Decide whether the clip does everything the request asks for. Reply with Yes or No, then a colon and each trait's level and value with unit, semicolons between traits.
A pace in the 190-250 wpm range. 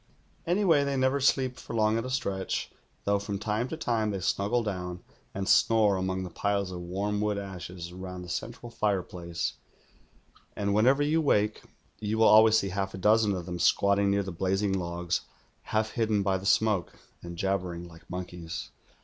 No: average, 180 wpm